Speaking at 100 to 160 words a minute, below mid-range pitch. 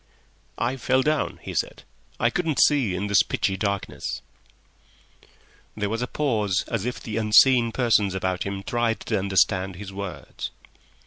Yes: average, 150 wpm; low, 105 Hz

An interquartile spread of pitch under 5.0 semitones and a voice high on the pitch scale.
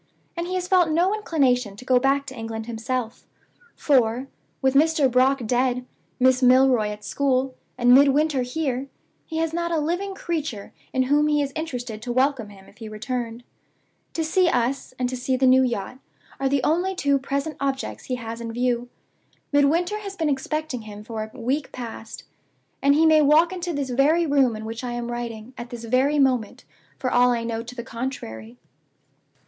Yes: average, 3.8 semitones; very high, 260 Hz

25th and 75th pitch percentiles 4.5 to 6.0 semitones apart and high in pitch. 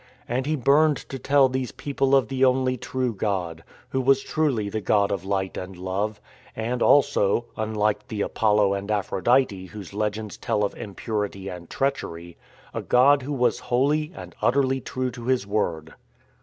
No: average, 4.8 semitones; low, 110 Hz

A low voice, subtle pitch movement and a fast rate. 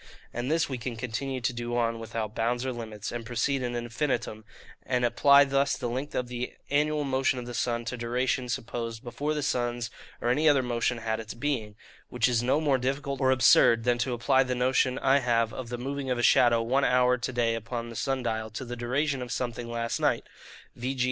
Yes: low, 125 Hz; narrow, 2.1 semitones; fast, 220 wpm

